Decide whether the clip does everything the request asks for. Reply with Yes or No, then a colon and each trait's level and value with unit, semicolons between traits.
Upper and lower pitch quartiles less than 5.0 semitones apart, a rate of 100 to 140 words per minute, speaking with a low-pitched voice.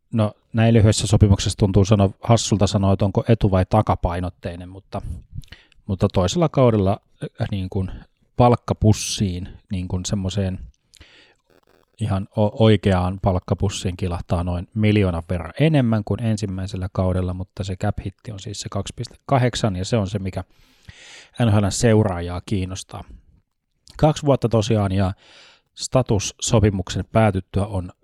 Yes: average, 2.8 semitones; average, 120 wpm; low, 100 Hz